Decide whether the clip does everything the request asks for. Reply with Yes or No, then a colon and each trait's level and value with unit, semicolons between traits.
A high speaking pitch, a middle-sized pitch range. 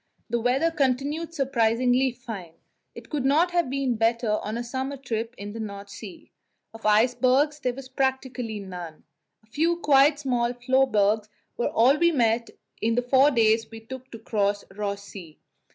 Yes: high, 245 Hz; average, 3.6 semitones